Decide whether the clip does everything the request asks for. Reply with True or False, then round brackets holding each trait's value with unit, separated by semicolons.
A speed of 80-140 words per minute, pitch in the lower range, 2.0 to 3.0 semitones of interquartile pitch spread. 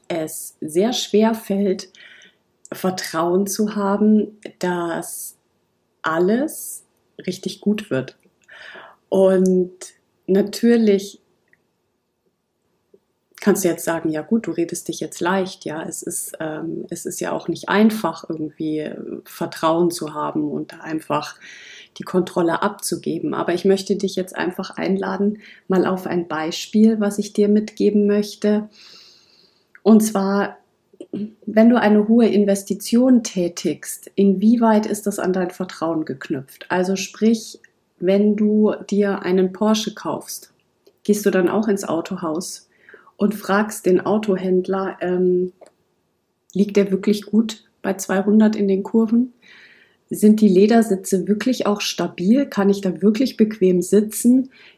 False (125 wpm; 195 Hz; 2.6 semitones)